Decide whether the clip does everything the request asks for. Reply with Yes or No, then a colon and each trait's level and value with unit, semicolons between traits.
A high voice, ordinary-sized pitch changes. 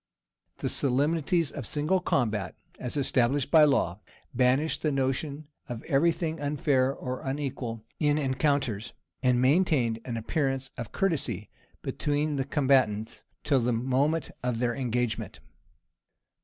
No: low, 135 Hz; average, 3.2 semitones